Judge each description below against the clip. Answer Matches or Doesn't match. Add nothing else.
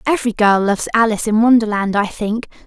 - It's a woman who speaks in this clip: Matches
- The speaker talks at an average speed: Matches